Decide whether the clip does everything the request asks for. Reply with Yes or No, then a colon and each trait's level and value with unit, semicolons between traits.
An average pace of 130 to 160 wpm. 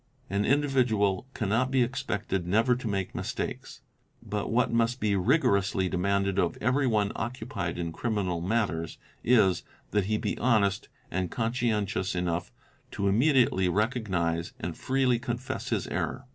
Yes: average, 140 wpm